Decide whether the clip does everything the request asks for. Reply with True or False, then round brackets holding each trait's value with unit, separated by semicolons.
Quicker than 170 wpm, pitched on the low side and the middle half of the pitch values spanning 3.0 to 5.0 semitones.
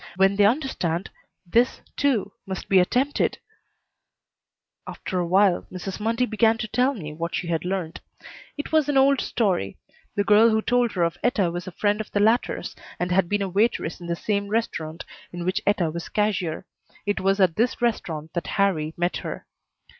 False (185 wpm; 200 Hz; 4.3 semitones)